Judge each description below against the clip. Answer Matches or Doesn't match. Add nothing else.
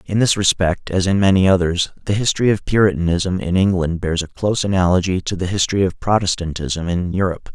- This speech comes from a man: Matches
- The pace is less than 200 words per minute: Matches